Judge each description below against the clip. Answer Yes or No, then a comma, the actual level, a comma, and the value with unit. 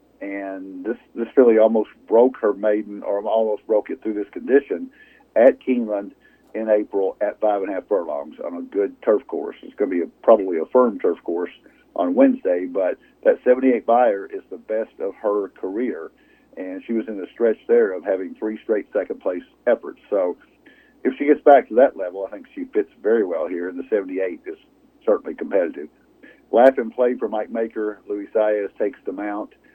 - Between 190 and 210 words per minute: Yes, average, 200 wpm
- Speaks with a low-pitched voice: Yes, low, 115 Hz